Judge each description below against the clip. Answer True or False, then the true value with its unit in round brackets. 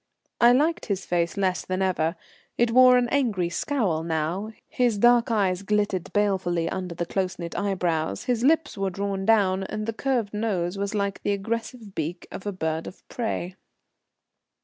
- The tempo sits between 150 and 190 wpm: True (170 wpm)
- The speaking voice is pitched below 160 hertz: False (200 Hz)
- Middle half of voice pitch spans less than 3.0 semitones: False (4.0 semitones)